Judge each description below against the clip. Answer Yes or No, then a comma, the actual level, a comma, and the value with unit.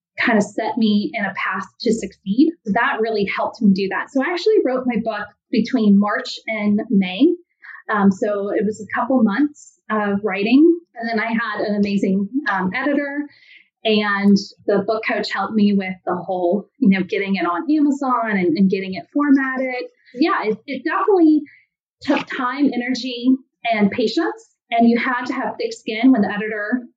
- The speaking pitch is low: No, high, 225 Hz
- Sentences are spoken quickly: No, average, 180 wpm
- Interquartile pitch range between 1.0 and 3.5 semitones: No, average, 4.8 semitones